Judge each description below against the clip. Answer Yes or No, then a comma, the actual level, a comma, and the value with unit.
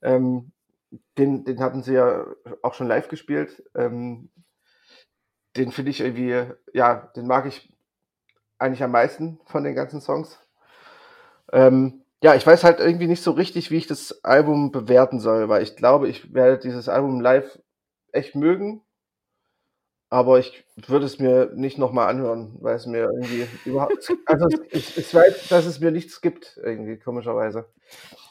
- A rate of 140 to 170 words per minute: Yes, average, 160 wpm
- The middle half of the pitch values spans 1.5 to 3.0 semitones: No, average, 4.8 semitones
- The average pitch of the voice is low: Yes, low, 130 Hz